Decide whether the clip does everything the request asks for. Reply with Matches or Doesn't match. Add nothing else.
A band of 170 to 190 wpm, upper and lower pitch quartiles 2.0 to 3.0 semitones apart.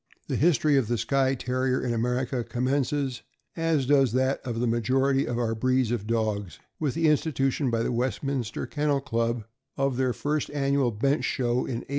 Matches